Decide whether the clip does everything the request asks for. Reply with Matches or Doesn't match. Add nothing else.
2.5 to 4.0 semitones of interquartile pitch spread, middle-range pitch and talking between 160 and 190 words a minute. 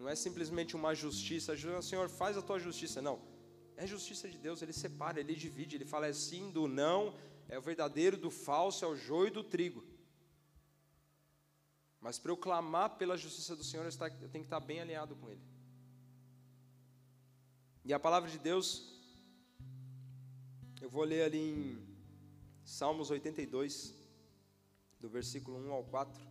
Doesn't match